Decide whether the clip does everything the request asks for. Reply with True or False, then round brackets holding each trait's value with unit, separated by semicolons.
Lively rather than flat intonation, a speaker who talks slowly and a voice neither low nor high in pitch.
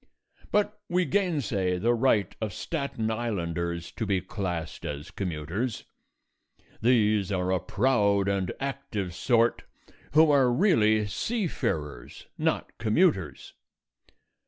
False (6.4 semitones; 110 wpm; 105 Hz)